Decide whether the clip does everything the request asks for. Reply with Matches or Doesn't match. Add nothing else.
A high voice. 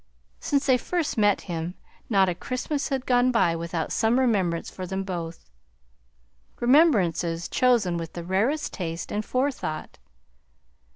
Matches